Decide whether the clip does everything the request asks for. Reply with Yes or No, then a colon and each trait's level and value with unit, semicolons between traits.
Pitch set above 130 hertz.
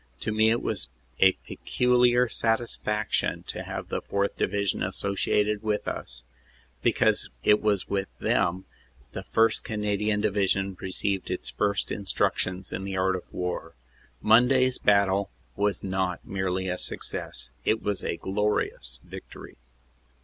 No: low, 100 Hz